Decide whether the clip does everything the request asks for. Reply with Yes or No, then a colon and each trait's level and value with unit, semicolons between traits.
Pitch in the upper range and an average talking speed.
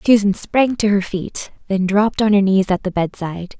No: high, 200 Hz; fast, 215 wpm